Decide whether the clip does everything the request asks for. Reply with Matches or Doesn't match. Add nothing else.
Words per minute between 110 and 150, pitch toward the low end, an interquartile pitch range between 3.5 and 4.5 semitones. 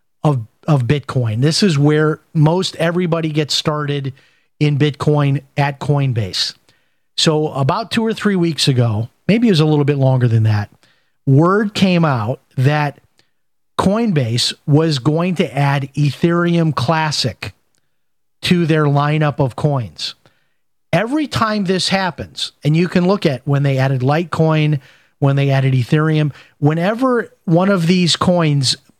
Doesn't match